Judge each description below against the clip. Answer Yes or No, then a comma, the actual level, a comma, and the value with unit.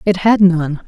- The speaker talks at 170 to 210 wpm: Yes, fast, 205 wpm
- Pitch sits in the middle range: Yes, medium, 180 Hz